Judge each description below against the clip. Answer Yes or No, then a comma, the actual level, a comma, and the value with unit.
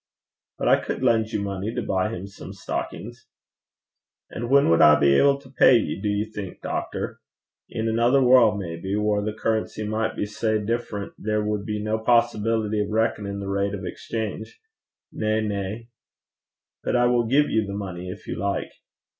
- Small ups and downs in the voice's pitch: Yes, narrow, 2.2 semitones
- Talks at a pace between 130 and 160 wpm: No, average, 185 wpm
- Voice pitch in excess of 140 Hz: No, low, 105 Hz